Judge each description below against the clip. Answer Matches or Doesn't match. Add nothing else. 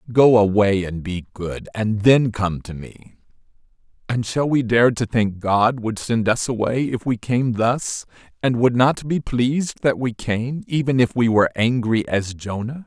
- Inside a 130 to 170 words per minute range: Doesn't match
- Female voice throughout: Doesn't match